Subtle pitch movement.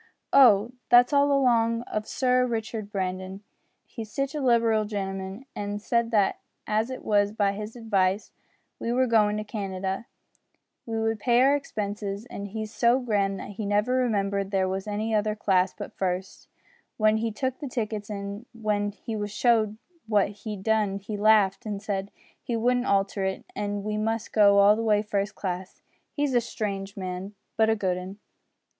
Yes: narrow, 2.3 semitones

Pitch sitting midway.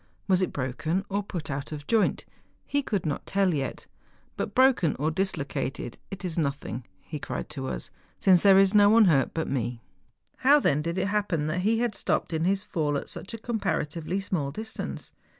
Yes: medium, 175 Hz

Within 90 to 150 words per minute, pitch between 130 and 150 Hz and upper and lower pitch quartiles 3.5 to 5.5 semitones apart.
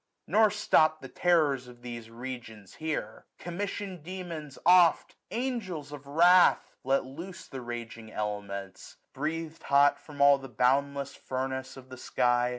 Yes: average, 145 wpm; medium, 140 Hz; average, 5.2 semitones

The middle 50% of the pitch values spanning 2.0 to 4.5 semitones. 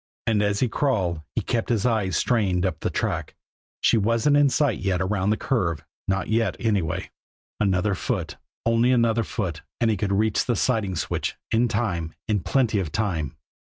Yes: average, 3.7 semitones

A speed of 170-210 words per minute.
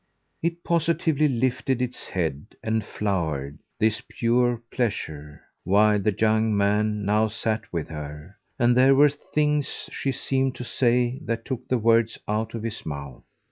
No: average, 150 wpm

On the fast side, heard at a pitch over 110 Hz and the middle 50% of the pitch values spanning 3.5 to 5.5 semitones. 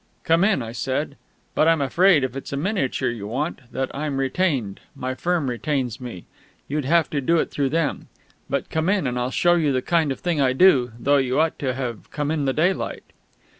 Yes: fast, 215 wpm; medium, 140 Hz; average, 4.0 semitones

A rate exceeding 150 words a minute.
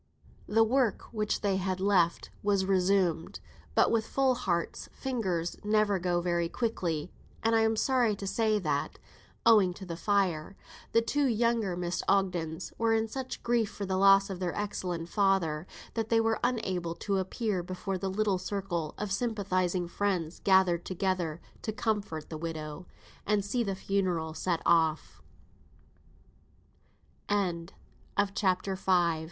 No: average, 145 wpm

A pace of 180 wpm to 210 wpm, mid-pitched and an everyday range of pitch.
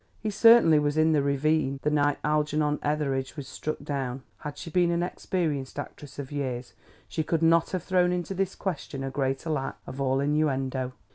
Yes: average, 190 wpm; medium, 150 Hz; average, 3.4 semitones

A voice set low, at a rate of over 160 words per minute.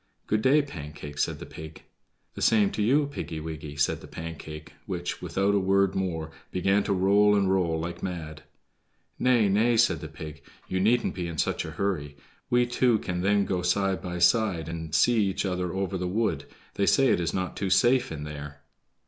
Yes: very low, 95 Hz; average, 200 wpm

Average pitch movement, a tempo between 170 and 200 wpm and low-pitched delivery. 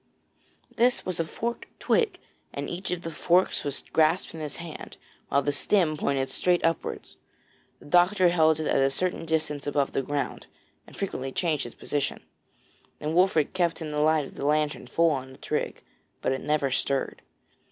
No: average, 3.5 semitones; average, 180 wpm; medium, 155 Hz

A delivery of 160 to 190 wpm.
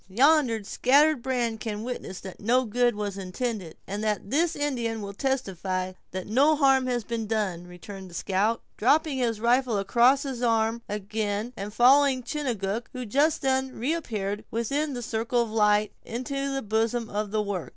Yes: average, 165 wpm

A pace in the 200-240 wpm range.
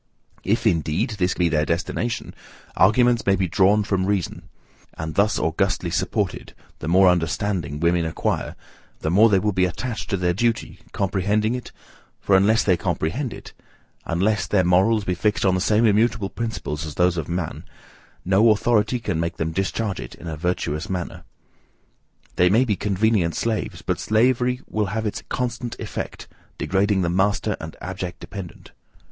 No: average, 165 wpm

